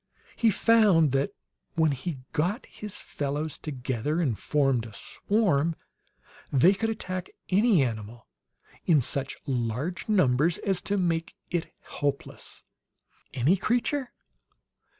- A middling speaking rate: No, slow, 115 wpm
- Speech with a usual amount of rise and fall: No, wide, 6.1 semitones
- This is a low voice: No, medium, 160 Hz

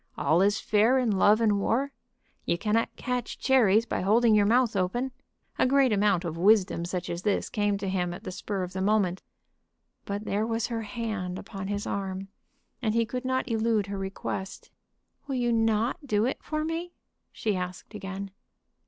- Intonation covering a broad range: No, average, 3.2 semitones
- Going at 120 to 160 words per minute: No, average, 185 wpm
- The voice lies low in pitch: No, high, 210 Hz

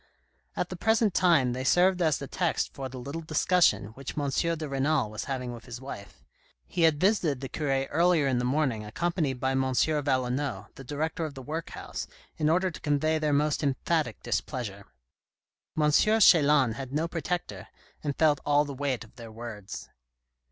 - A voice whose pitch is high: No, medium, 145 Hz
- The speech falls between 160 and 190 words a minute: Yes, average, 180 wpm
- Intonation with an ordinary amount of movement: Yes, average, 3.8 semitones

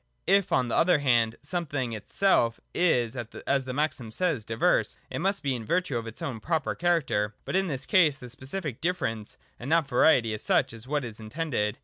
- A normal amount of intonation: No, wide, 6.2 semitones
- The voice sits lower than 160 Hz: Yes, low, 135 Hz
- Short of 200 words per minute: No, fast, 205 wpm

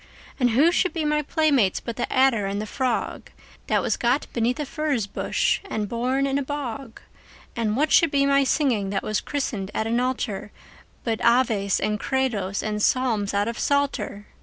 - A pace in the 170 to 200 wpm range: Yes, average, 185 wpm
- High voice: Yes, high, 245 Hz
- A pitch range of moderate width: Yes, average, 4.6 semitones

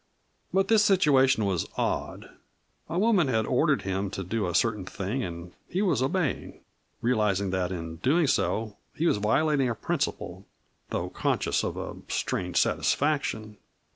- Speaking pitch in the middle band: No, low, 115 Hz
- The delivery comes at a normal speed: Yes, average, 150 wpm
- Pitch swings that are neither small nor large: No, wide, 7.9 semitones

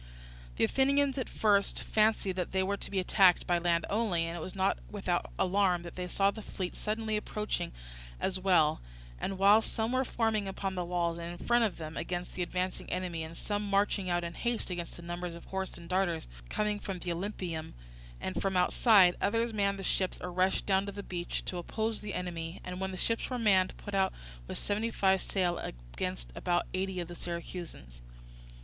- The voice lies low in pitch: No, medium, 185 Hz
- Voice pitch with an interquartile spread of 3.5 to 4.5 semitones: No, average, 2.8 semitones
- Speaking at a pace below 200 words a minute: No, fast, 205 wpm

